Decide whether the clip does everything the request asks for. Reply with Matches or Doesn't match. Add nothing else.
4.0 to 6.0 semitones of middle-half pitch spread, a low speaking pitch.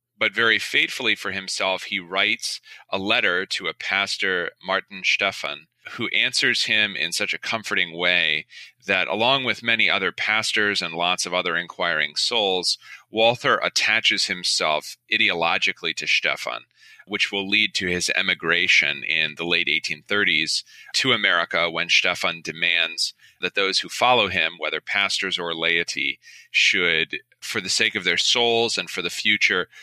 Matches